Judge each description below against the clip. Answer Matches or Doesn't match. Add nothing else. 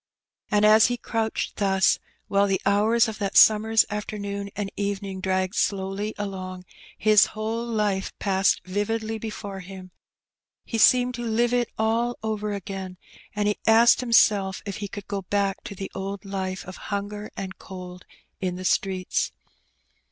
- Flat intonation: Matches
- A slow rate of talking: Doesn't match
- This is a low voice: Doesn't match